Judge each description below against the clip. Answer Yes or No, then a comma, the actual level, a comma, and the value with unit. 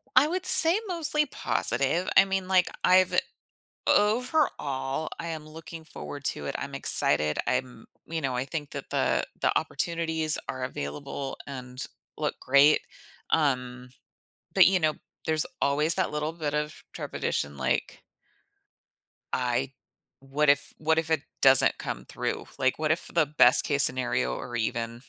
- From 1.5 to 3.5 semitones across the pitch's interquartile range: No, average, 4.2 semitones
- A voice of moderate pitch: Yes, medium, 150 Hz